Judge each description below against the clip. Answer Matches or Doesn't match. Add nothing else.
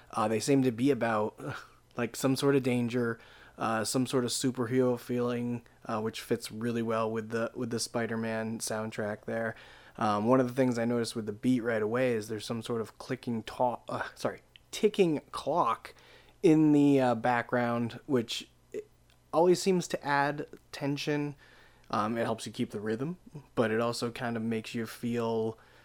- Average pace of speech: Matches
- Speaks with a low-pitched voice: Matches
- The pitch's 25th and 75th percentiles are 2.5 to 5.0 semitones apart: Matches